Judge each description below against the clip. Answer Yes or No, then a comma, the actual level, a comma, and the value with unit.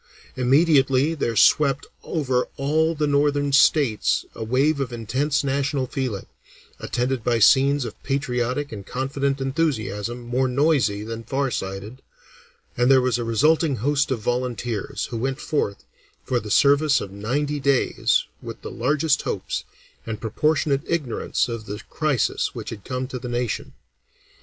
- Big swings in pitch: No, average, 3.3 semitones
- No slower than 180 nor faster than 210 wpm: No, average, 145 wpm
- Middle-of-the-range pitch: No, low, 130 Hz